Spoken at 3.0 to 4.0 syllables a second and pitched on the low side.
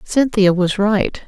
No: 3.5 syllables/s; high, 200 Hz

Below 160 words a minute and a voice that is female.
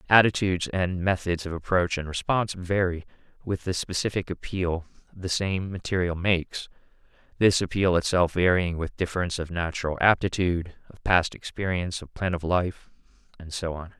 No: average, 150 wpm; male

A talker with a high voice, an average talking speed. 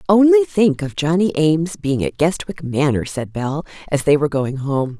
No: medium, 160 Hz; average, 190 wpm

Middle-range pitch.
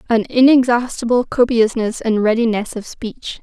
No: high, 235 Hz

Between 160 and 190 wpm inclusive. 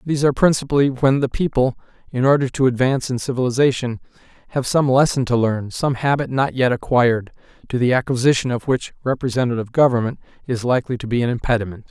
Yes: average, 175 wpm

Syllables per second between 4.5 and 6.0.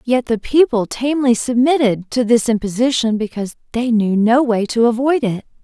Yes: 5.2 syllables/s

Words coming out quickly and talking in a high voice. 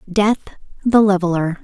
No: slow, 110 wpm; high, 195 Hz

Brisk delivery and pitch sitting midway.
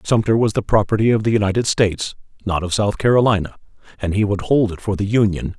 No: fast, 215 wpm; low, 105 Hz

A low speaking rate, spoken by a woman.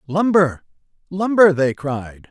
No: slow, 105 wpm; male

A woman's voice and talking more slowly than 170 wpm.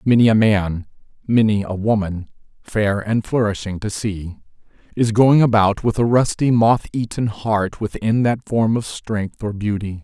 No: male; average, 160 wpm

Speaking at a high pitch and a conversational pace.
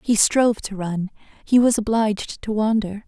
Yes: high, 215 Hz; average, 175 wpm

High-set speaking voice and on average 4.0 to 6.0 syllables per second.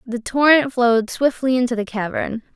Yes: high, 245 Hz; 5.1 syllables/s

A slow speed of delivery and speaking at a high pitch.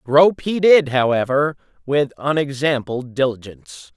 No: slow, 105 wpm; medium, 140 Hz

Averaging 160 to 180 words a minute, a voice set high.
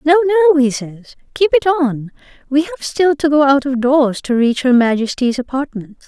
No: average, 200 wpm; very high, 280 Hz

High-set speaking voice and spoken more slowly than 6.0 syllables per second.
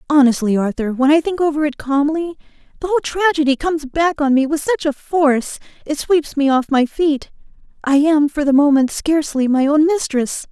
Yes: very high, 290 Hz; 5.4 syllables/s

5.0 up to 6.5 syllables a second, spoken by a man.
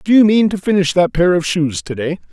Yes: 5.6 syllables/s; male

